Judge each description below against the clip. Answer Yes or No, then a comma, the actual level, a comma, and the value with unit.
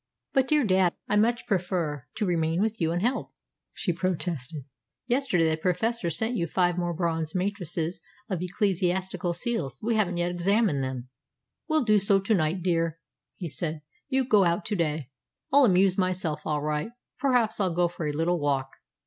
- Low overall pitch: No, medium, 180 Hz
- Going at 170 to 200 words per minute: Yes, average, 180 wpm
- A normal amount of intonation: Yes, average, 4.2 semitones